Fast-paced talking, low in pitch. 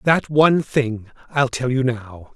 No: average, 180 wpm; low, 130 Hz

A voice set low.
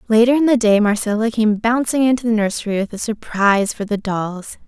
No: high, 220 Hz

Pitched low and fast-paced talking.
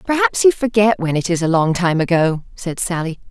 No: medium, 185 Hz; fast, 220 wpm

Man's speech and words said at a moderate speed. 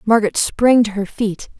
No: female; average, 190 wpm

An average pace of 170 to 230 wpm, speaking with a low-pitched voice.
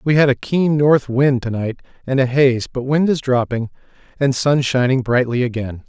Yes: fast, 205 wpm; low, 130 Hz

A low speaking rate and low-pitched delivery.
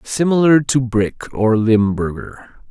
Yes: slow, 110 wpm; low, 120 Hz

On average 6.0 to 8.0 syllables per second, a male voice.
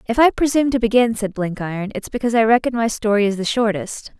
No: 6.5 syllables/s; female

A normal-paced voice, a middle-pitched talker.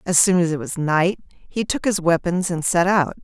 No: fast, 240 wpm; medium, 175 Hz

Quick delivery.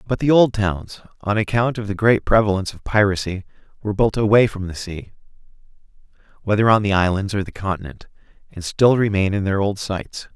No: average, 185 wpm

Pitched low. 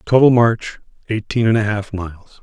Yes: low, 110 Hz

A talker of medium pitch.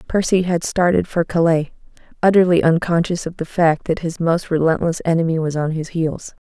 Yes: medium, 170 Hz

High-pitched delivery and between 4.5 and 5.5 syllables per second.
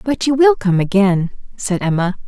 Yes: high, 210 Hz; 4.9 syllables/s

